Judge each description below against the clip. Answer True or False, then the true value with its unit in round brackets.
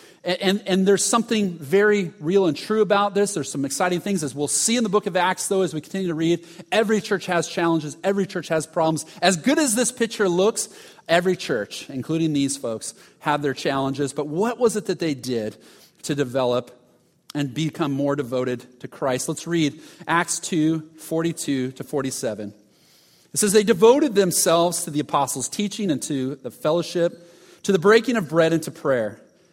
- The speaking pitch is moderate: True (170 Hz)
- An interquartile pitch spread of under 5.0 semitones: False (5.4 semitones)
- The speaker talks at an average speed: True (190 wpm)